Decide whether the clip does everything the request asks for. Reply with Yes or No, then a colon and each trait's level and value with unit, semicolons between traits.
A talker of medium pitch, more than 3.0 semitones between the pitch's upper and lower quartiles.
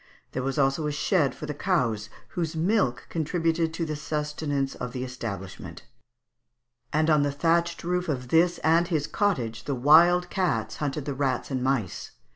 Yes: medium, 150 Hz; average, 4.6 semitones